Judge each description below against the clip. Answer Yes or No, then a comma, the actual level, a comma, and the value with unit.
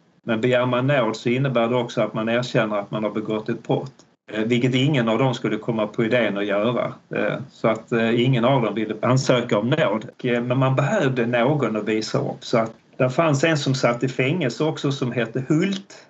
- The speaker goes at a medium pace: No, fast, 210 wpm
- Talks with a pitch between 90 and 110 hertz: No, low, 125 Hz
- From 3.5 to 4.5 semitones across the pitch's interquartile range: No, average, 3.1 semitones